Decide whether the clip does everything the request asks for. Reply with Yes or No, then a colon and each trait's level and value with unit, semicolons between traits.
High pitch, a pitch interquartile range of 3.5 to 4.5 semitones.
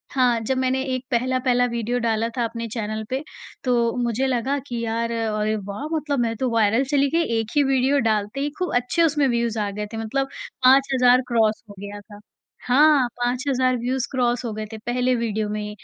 No: high, 245 Hz; average, 2.7 semitones